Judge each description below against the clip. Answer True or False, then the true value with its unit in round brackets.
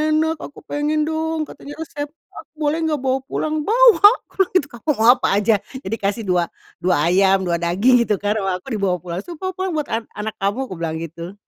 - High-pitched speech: True (235 Hz)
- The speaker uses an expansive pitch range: True (8.2 semitones)